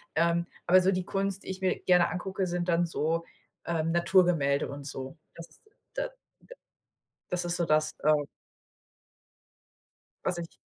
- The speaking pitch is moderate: Yes, medium, 175 Hz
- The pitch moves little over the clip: Yes, narrow, 2.0 semitones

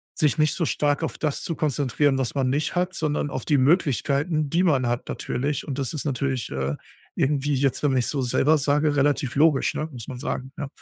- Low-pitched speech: No, medium, 145 Hz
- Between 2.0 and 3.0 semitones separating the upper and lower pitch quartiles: Yes, narrow, 2.5 semitones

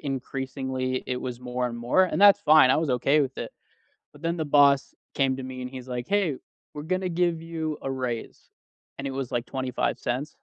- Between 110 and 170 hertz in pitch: Yes, low, 135 Hz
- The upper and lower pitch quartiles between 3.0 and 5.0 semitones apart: Yes, average, 3.6 semitones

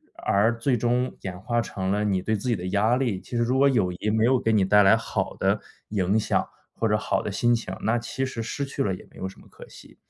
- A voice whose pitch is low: Yes, low, 110 Hz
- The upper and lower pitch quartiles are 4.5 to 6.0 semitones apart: No, average, 3.5 semitones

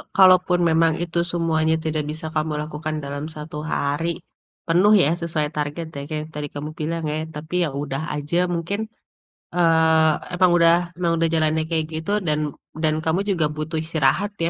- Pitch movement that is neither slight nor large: No, narrow, 1.7 semitones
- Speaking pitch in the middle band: Yes, medium, 160 Hz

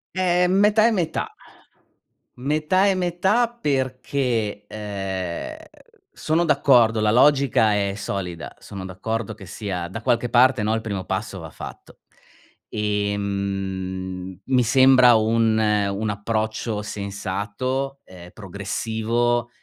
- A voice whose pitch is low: Yes, low, 110 Hz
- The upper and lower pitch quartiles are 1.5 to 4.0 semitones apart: No, average, 4.9 semitones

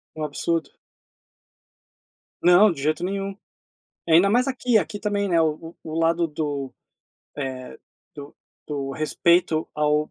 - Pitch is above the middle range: No, medium, 165 Hz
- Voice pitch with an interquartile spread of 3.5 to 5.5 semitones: Yes, average, 4.2 semitones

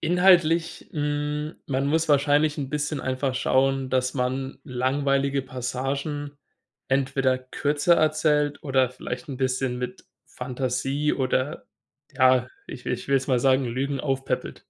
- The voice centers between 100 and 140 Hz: Yes, low, 135 Hz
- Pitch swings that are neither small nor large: No, narrow, 2.2 semitones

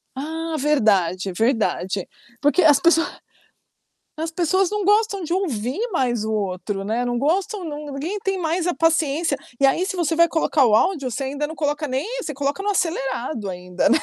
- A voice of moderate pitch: No, very high, 295 Hz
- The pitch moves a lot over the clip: Yes, wide, 5.8 semitones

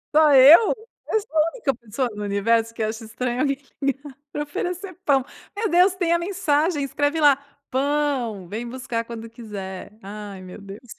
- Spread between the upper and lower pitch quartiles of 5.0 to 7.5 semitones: Yes, average, 5.3 semitones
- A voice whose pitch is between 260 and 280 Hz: Yes, very high, 265 Hz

